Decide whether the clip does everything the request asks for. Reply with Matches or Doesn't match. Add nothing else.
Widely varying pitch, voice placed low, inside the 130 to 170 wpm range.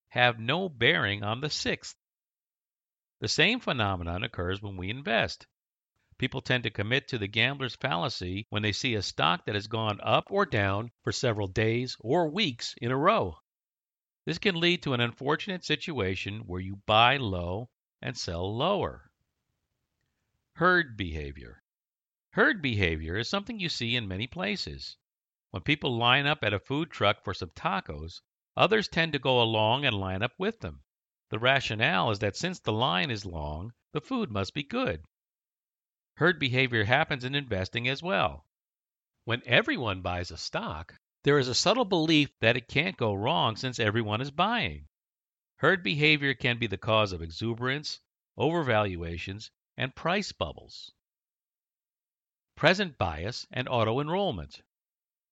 Matches